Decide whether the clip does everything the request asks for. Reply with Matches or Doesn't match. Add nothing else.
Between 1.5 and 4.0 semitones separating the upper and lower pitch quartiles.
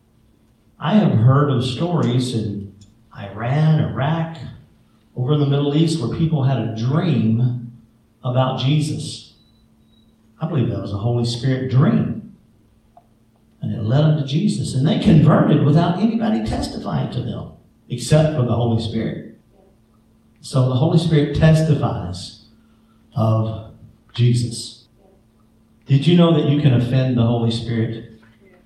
Doesn't match